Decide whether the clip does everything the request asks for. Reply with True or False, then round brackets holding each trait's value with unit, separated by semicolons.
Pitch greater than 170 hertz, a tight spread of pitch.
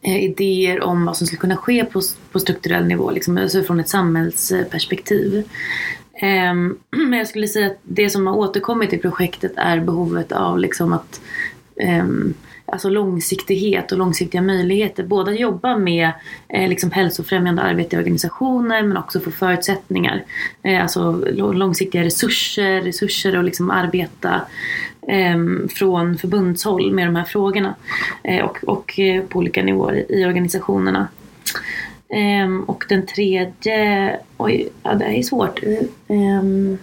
True (190 Hz; 2.0 semitones)